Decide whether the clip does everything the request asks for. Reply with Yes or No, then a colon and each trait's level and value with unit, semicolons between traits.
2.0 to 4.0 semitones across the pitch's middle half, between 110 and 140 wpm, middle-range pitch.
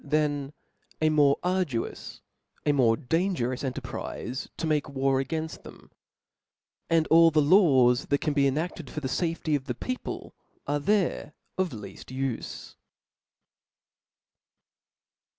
Yes: average, 3.6 semitones; slow, 135 wpm; medium, 145 Hz